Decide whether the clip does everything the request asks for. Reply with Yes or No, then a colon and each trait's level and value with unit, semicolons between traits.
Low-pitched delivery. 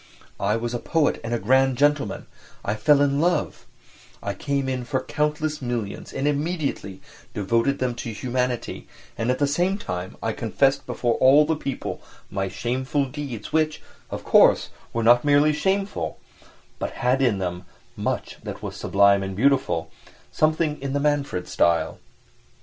Yes: low, 130 Hz